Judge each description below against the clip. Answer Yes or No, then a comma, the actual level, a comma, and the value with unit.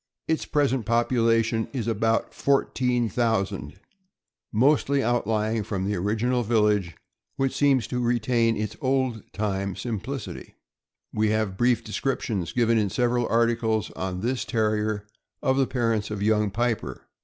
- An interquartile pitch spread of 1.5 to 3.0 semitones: Yes, narrow, 2.6 semitones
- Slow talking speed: Yes, slow, 130 wpm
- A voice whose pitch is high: No, low, 115 Hz